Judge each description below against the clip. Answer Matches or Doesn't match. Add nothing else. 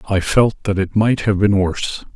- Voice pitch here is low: Matches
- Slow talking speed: Doesn't match